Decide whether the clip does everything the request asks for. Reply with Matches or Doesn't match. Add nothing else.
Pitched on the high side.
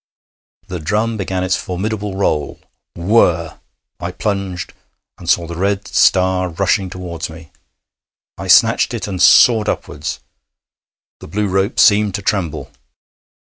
Doesn't match